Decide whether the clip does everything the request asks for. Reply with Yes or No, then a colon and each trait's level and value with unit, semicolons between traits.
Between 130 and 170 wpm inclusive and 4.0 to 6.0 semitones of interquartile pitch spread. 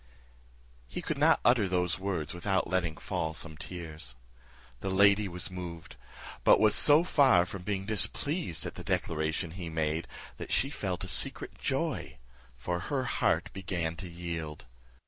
No: average, 150 wpm; average, 3.4 semitones